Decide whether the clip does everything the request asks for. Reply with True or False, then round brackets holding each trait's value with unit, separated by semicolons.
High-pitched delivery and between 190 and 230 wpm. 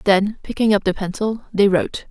True (200 Hz; 200 wpm)